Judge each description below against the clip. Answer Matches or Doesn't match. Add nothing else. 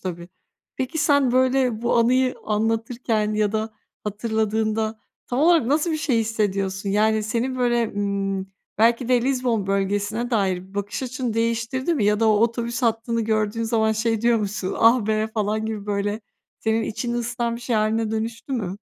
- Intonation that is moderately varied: Doesn't match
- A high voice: Matches